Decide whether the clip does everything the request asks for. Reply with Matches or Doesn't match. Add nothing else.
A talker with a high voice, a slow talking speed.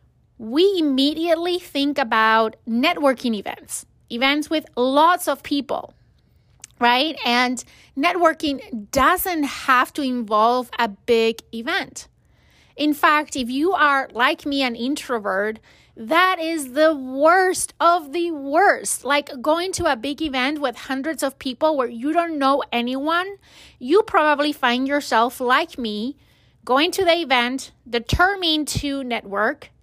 Matches